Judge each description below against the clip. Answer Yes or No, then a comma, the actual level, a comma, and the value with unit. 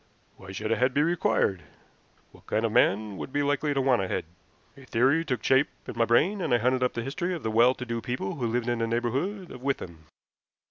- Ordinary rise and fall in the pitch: Yes, average, 3.6 semitones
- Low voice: Yes, low, 125 Hz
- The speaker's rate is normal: No, fast, 240 wpm